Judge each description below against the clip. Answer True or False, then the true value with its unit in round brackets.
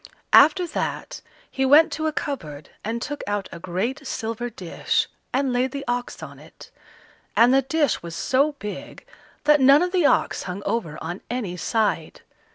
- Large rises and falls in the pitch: True (5.7 semitones)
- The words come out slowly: False (170 wpm)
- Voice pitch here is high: True (245 Hz)